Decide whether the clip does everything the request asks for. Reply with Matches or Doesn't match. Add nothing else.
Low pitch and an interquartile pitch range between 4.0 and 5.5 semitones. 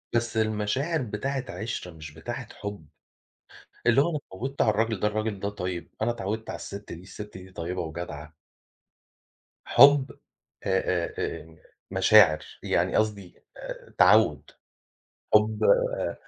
Matches